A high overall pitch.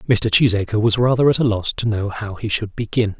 No: low, 110 Hz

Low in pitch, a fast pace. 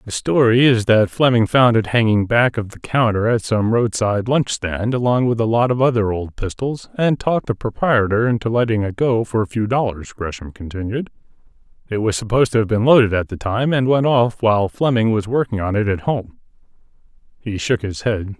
Yes: low, 115 Hz; fast, 210 wpm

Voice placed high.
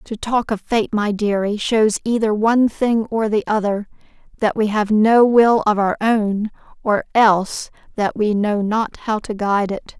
Yes: high, 215 Hz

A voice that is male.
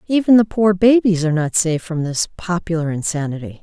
No: female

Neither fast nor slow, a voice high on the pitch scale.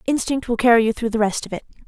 No: fast, 290 wpm; high, 230 Hz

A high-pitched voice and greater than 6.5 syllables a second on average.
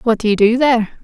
Yes: high, 230 Hz; 7.3 syllables/s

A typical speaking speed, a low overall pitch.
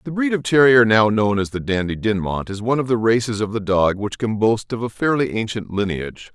No: fast, 245 wpm; low, 110 Hz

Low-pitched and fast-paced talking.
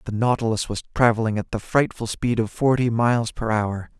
No: low, 115 Hz; average, 195 wpm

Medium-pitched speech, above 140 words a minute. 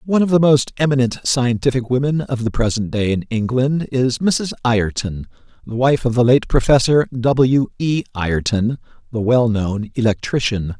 No: low, 125 Hz; average, 155 wpm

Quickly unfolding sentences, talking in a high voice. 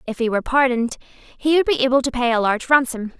Yes: fast, 245 wpm; very high, 250 Hz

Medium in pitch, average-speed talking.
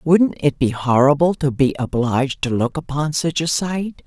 Yes: medium, 145 Hz; average, 190 wpm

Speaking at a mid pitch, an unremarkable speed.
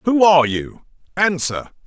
No: medium, 160 Hz; slow, 130 wpm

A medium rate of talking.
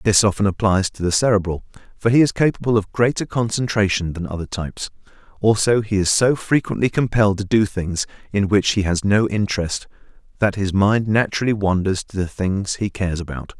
Yes: average, 185 wpm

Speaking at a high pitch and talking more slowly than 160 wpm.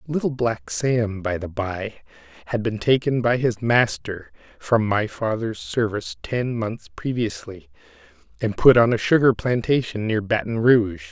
No: low, 115 Hz; average, 150 wpm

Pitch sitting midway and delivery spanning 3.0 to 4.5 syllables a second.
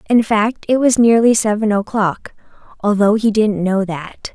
No: high, 210 Hz; 4.4 syllables/s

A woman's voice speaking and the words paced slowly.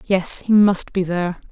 No: female; average, 200 wpm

